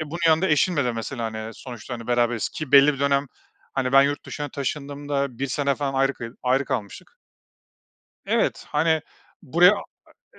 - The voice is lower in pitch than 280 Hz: Yes, medium, 140 Hz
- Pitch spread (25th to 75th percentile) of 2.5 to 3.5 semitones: Yes, average, 2.9 semitones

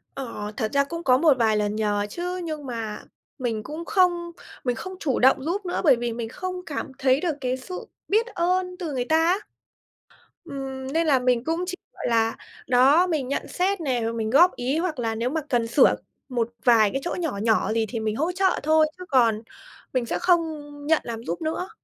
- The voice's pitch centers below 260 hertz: No, very high, 270 Hz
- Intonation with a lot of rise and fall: Yes, wide, 6.5 semitones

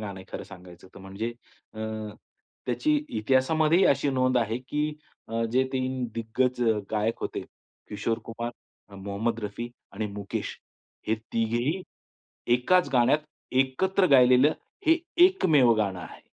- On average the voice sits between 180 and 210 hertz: No, low, 120 Hz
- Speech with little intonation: No, average, 3.4 semitones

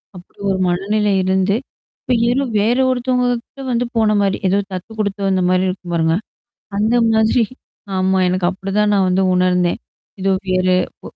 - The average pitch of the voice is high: Yes, high, 195 Hz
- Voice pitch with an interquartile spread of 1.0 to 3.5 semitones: Yes, average, 3.1 semitones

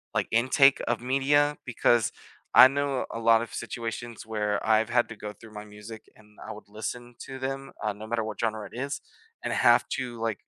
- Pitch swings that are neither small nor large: Yes, average, 3.1 semitones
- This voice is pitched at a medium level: No, low, 115 Hz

